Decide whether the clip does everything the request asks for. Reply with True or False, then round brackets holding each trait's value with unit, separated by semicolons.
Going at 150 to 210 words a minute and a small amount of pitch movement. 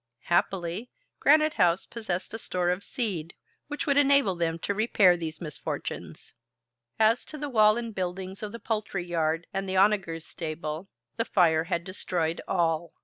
False (160 wpm; 4.4 semitones)